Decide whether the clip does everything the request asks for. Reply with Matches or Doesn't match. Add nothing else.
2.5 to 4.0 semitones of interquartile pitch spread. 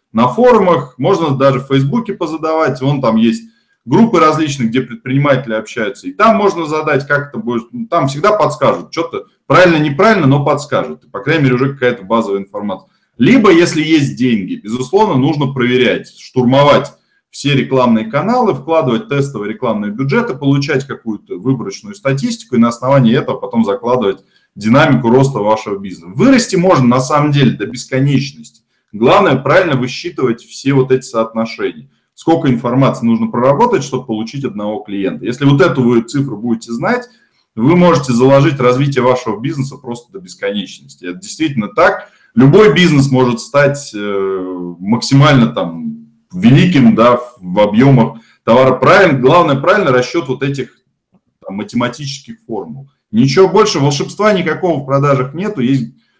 Doesn't match